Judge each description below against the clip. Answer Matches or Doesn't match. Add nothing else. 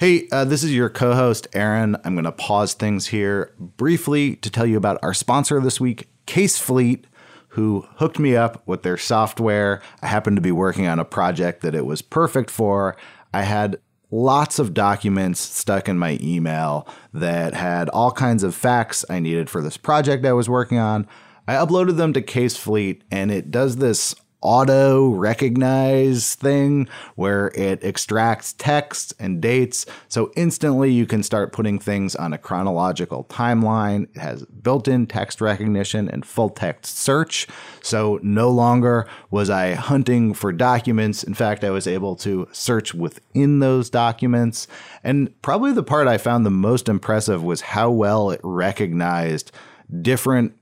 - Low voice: Matches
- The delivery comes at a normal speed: Matches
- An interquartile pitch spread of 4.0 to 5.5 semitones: Matches